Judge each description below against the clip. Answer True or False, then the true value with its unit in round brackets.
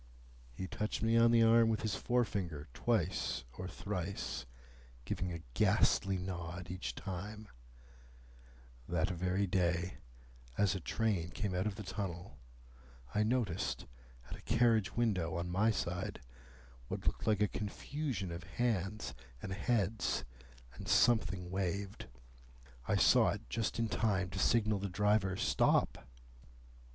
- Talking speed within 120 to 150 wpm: True (135 wpm)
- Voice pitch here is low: True (95 Hz)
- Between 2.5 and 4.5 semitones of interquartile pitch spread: True (3.5 semitones)